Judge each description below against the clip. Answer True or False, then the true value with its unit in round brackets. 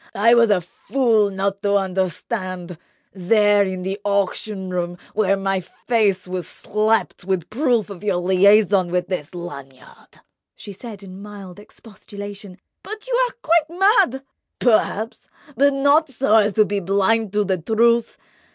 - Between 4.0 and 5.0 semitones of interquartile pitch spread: False (3.2 semitones)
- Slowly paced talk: False (145 wpm)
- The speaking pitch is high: True (200 Hz)